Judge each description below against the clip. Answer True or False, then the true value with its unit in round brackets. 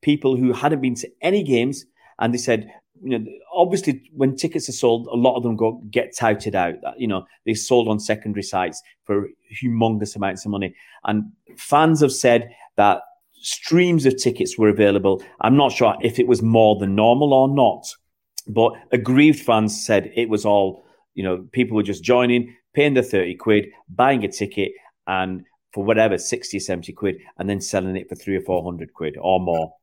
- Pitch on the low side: True (115 Hz)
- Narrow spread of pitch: False (4.1 semitones)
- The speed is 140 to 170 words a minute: False (195 wpm)